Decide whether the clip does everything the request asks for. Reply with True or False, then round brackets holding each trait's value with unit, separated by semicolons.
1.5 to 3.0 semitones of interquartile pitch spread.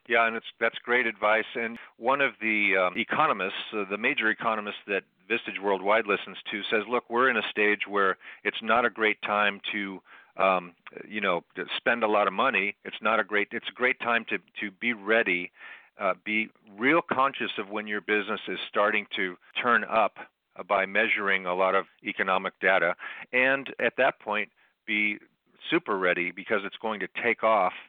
True (2.5 semitones)